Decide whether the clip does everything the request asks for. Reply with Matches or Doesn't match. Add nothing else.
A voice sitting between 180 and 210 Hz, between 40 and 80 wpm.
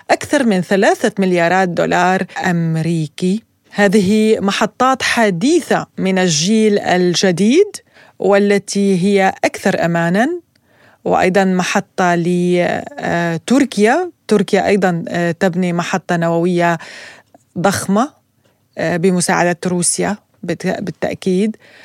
Matches